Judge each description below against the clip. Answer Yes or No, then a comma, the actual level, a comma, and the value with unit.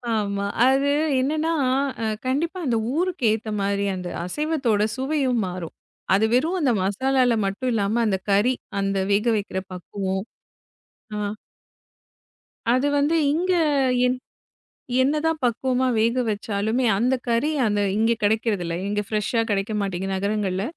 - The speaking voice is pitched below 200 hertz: No, high, 225 Hz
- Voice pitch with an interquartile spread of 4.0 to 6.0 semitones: Yes, average, 4.7 semitones